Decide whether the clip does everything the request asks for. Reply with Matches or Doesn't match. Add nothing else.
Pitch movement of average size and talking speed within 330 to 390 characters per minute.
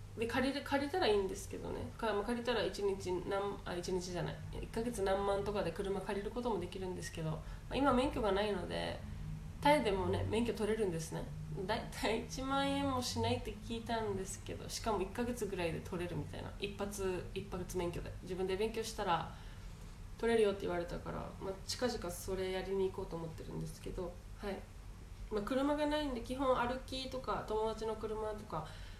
Matches